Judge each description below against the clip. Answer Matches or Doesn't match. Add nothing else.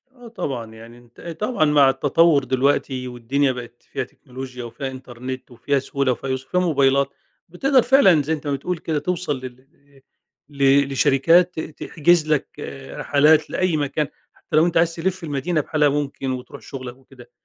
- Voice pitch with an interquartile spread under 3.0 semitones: Doesn't match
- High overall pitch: Doesn't match